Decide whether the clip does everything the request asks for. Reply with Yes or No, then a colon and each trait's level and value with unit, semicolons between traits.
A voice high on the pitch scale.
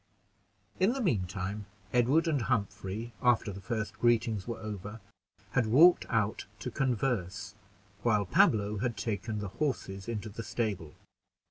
No: low, 110 Hz